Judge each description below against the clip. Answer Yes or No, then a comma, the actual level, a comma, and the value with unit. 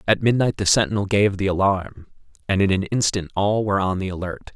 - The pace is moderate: No, fast, 210 wpm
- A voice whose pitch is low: Yes, low, 100 Hz